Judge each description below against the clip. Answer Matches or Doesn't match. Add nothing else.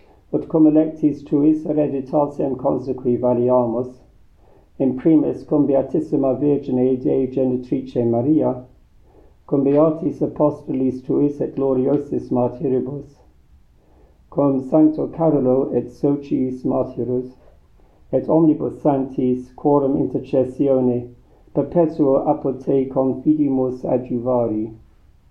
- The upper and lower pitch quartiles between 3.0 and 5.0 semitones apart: Doesn't match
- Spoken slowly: Matches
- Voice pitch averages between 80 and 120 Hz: Doesn't match